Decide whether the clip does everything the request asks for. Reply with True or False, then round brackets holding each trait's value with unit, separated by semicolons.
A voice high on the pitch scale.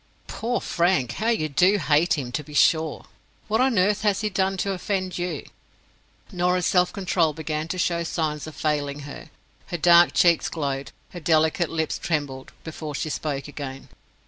False (165 Hz)